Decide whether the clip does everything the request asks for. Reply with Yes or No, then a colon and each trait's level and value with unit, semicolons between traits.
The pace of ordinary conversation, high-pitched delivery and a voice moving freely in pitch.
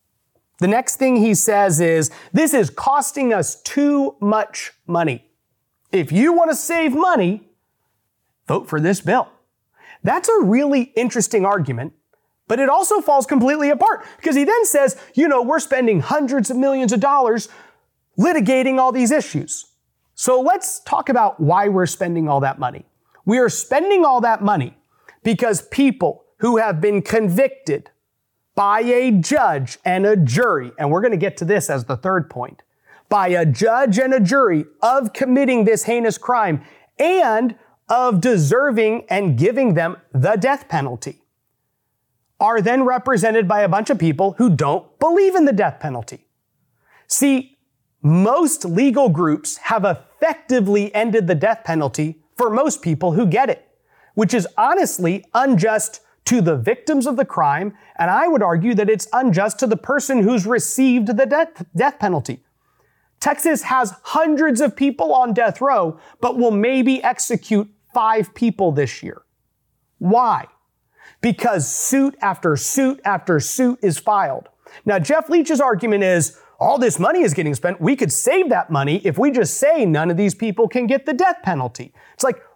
Yes: average, 160 wpm; high, 225 Hz; wide, 7.5 semitones